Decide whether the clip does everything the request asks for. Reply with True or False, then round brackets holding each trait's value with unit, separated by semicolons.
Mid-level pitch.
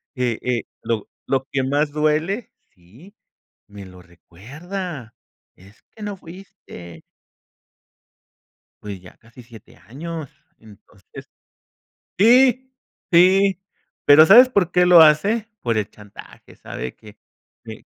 True (145 Hz)